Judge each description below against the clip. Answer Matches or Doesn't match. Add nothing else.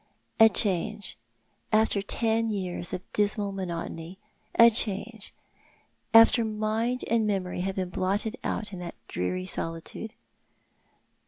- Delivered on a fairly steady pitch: Doesn't match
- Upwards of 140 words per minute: Doesn't match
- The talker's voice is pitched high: Matches